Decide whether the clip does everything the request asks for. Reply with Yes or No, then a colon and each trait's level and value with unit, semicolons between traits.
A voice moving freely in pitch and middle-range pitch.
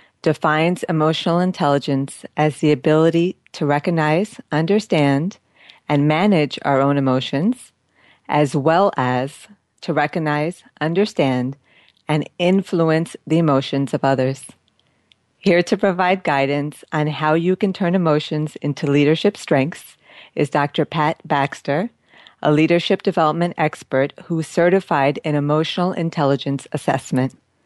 No: average, 3.5 semitones; medium, 155 Hz